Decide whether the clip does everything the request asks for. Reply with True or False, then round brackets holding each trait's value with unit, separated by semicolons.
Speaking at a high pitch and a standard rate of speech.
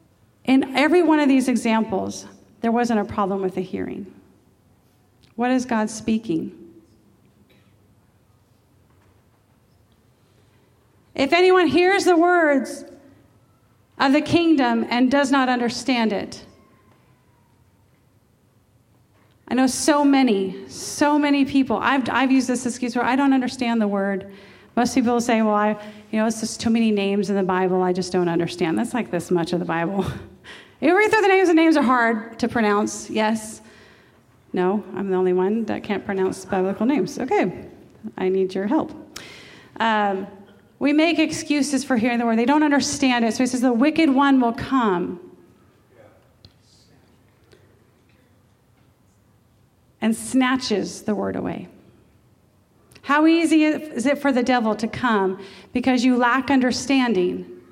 True (225 Hz; 145 wpm)